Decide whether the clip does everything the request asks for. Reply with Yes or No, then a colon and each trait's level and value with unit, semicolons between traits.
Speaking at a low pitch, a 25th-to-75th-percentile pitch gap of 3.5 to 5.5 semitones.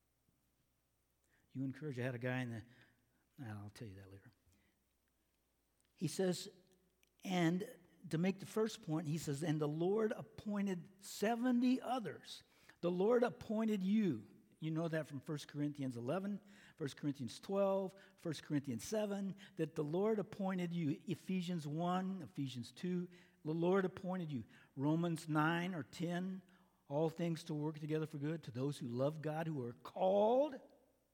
No: medium, 165 Hz; average, 5.1 semitones